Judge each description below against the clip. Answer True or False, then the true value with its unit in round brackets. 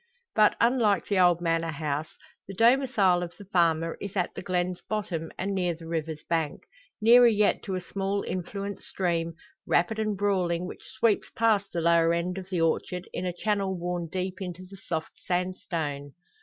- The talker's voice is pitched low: False (180 Hz)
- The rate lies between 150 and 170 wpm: False (180 wpm)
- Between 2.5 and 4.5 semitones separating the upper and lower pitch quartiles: True (3.1 semitones)